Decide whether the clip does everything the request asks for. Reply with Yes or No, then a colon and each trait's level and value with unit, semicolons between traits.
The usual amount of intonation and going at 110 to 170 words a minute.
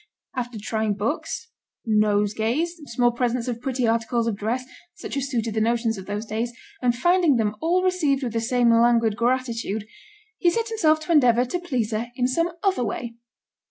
No: average, 3.6 semitones; average, 180 wpm